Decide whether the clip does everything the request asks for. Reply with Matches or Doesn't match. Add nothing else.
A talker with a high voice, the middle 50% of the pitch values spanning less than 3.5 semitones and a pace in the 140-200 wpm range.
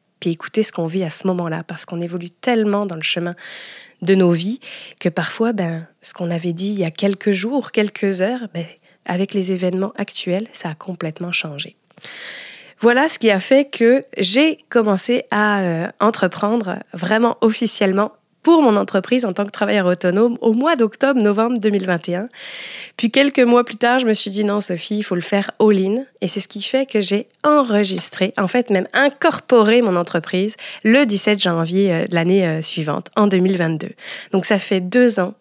Doesn't match